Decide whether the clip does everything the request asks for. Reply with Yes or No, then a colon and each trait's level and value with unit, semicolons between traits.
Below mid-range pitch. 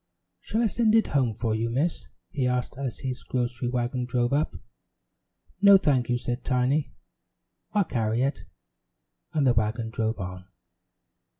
Yes: low, 125 Hz